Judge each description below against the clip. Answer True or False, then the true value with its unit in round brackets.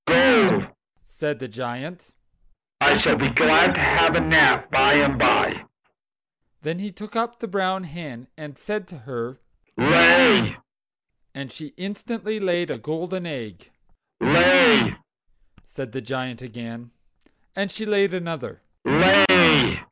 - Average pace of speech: False (130 wpm)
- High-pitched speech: False (160 Hz)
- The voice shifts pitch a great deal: True (7.2 semitones)